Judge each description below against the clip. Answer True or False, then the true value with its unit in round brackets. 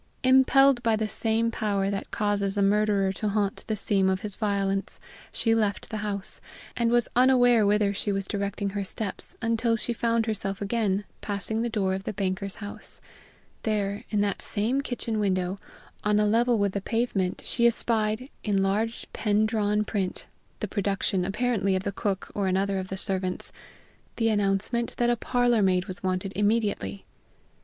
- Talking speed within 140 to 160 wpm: False (175 wpm)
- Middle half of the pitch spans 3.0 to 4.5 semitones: False (2.5 semitones)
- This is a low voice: False (205 Hz)